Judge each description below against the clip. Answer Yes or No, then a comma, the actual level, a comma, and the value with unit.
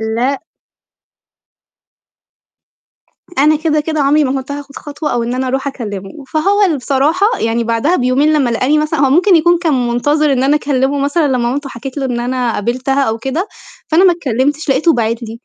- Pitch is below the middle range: No, very high, 275 Hz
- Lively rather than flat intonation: No, average, 3.6 semitones